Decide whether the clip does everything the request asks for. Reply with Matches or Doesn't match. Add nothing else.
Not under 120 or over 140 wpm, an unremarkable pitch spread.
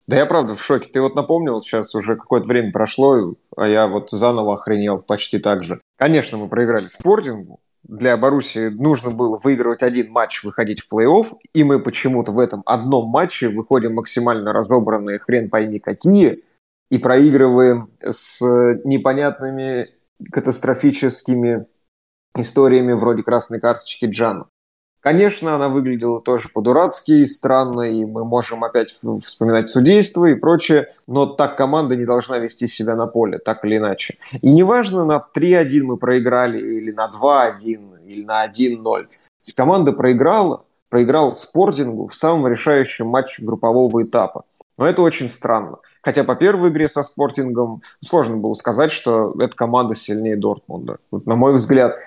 Doesn't match